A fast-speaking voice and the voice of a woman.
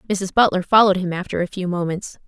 Yes: fast, 210 wpm; female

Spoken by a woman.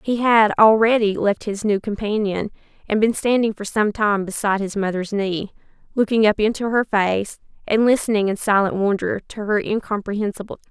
Yes: female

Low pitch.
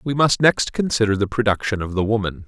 Yes: low, 110 Hz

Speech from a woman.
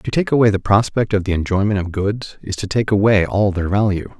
No: male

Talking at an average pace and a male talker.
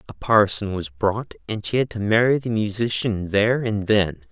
Yes: average, 195 wpm; male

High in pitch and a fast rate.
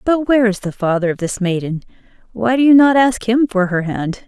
Yes: high, 215 Hz; fast, 225 wpm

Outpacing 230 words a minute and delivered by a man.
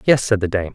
Yes: fast, 320 wpm; male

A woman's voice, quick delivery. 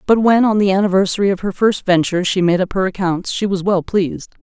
Yes: female; fast, 245 wpm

